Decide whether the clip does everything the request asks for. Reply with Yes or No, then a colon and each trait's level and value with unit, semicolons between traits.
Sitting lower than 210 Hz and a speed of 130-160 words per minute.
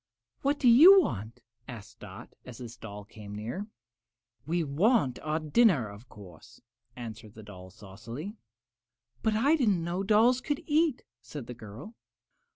Yes: medium, 140 Hz; average, 150 wpm